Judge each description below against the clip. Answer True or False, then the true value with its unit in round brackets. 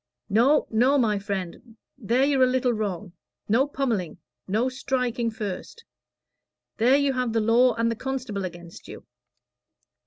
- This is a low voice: False (235 Hz)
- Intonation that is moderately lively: True (3.7 semitones)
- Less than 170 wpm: True (145 wpm)